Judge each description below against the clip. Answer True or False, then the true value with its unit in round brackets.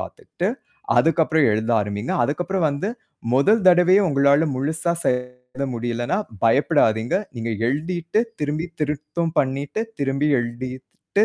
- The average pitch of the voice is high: False (145 Hz)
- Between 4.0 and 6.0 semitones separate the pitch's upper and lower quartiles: True (5.2 semitones)